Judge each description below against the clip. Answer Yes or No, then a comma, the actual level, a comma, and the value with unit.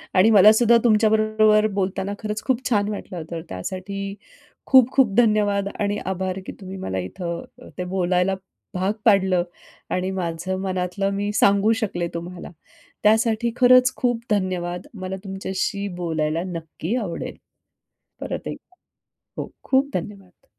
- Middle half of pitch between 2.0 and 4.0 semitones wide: Yes, average, 2.9 semitones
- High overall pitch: Yes, high, 195 Hz